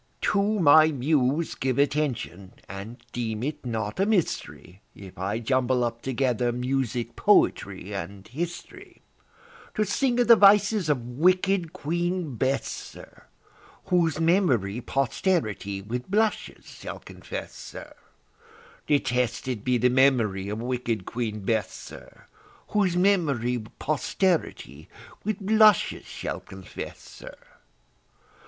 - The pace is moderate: No, slow, 115 wpm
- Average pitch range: No, wide, 7.3 semitones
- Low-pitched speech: Yes, low, 130 Hz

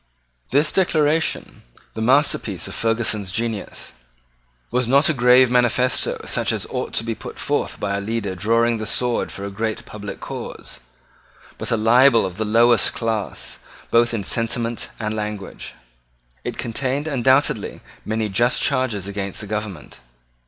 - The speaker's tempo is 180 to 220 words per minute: No, average, 150 wpm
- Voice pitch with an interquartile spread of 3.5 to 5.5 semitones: No, average, 2.7 semitones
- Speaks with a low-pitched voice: Yes, low, 115 Hz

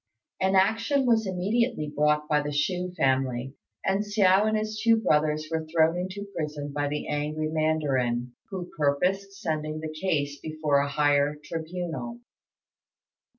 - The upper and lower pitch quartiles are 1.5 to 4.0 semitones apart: No, average, 4.5 semitones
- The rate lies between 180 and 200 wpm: No, average, 145 wpm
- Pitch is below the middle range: No, medium, 155 Hz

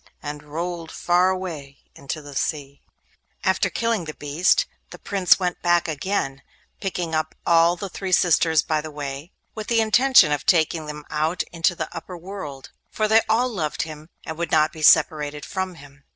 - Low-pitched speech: No, medium, 165 Hz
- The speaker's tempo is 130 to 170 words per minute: No, average, 180 wpm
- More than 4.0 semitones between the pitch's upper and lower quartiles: No, average, 3.7 semitones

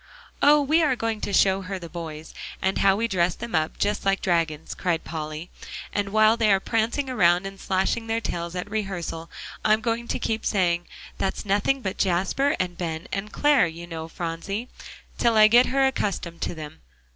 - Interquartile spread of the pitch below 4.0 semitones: No, average, 4.7 semitones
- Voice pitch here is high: Yes, high, 195 Hz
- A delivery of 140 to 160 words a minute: No, average, 190 wpm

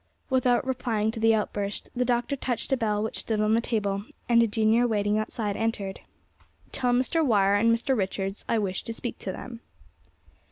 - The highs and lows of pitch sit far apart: No, average, 2.8 semitones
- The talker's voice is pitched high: Yes, high, 225 Hz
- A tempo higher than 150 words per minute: Yes, average, 190 wpm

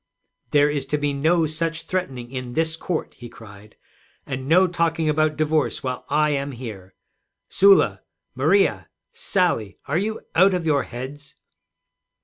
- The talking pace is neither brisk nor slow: Yes, average, 145 wpm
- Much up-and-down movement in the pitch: No, average, 4.3 semitones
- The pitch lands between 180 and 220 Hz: No, medium, 150 Hz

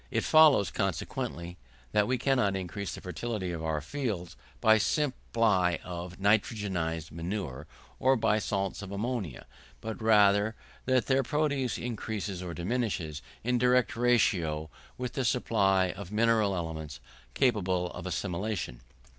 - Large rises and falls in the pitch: No, average, 5.0 semitones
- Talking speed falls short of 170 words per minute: Yes, average, 140 wpm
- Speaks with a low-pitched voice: Yes, low, 100 Hz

